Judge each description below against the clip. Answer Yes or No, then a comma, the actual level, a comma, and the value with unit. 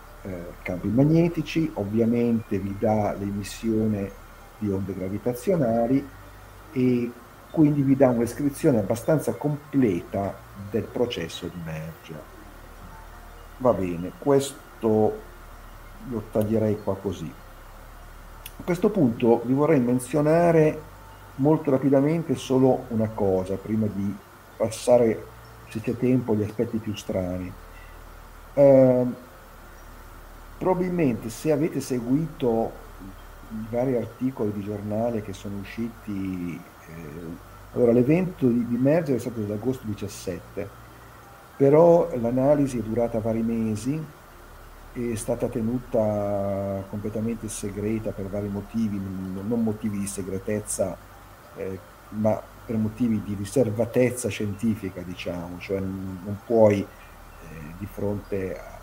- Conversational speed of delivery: No, slow, 110 wpm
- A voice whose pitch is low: Yes, low, 110 Hz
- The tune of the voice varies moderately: Yes, average, 4.1 semitones